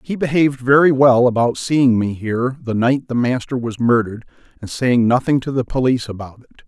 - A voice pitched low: Yes, low, 125 Hz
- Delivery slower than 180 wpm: No, average, 200 wpm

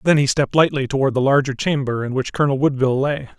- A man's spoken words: Yes, male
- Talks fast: Yes, fast, 230 wpm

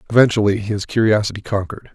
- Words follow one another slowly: Yes, slow, 125 wpm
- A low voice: Yes, low, 105 Hz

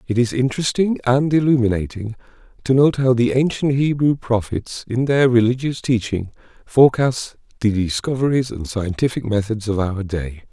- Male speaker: Yes, male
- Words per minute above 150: No, average, 145 wpm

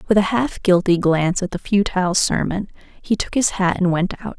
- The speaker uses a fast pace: Yes, fast, 220 wpm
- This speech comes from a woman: Yes, female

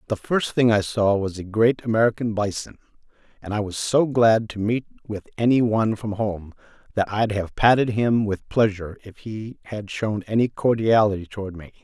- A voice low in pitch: Yes, low, 110 Hz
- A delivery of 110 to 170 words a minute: No, average, 190 wpm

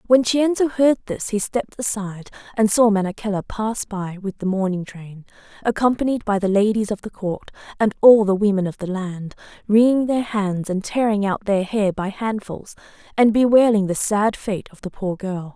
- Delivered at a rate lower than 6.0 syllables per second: Yes, 5.0 syllables/s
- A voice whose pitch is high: Yes, high, 205 Hz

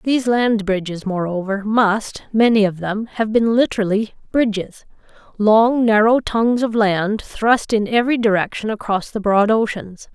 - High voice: Yes, high, 215 Hz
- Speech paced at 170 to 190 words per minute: No, average, 150 wpm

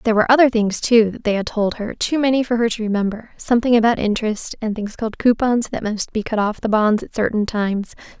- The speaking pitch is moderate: No, high, 220 Hz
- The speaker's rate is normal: No, fast, 225 wpm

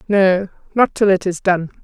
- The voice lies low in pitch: No, high, 190 Hz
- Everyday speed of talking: Yes, average, 195 wpm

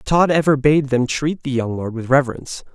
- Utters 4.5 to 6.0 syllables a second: Yes, 5.5 syllables/s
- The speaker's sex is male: Yes, male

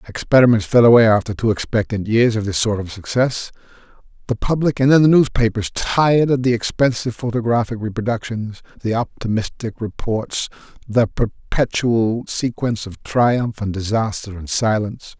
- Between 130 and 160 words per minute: Yes, average, 140 wpm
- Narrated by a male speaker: Yes, male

